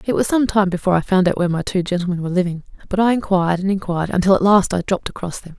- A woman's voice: Yes, female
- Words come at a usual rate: No, fast, 280 wpm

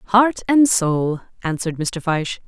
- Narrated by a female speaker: Yes, female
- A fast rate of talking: No, average, 145 wpm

